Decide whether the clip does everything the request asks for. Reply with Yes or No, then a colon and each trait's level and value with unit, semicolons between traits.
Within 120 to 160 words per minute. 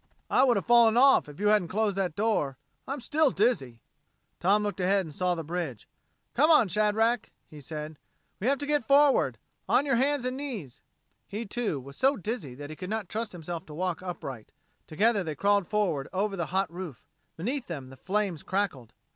No: average, 195 wpm